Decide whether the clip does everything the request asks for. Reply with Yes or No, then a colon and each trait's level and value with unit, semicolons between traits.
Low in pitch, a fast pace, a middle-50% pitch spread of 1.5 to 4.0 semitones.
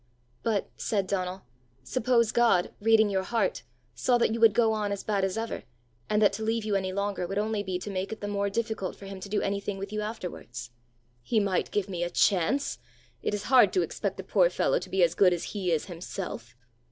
No: high, 200 Hz; fast, 225 wpm; average, 2.8 semitones